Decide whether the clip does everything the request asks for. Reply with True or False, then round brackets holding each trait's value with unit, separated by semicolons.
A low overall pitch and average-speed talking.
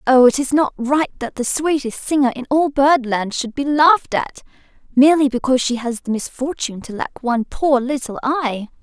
False (265 Hz; 190 wpm)